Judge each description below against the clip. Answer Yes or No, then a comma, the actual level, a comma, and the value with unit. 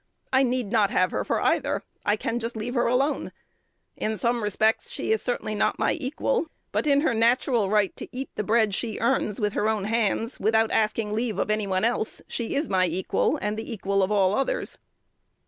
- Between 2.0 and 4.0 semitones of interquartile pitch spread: Yes, average, 2.9 semitones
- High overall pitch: Yes, high, 220 Hz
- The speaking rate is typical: No, fast, 210 wpm